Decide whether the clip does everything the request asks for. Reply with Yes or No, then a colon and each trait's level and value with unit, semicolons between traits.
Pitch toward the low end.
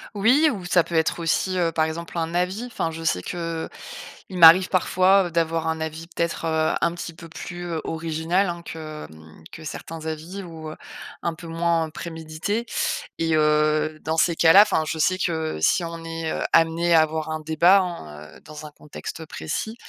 No: medium, 165 Hz